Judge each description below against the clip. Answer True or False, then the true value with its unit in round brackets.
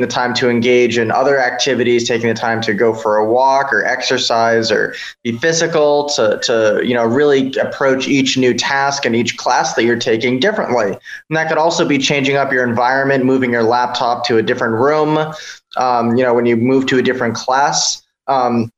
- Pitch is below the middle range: True (125 Hz)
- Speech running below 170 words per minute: False (200 wpm)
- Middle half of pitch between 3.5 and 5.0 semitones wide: False (2.8 semitones)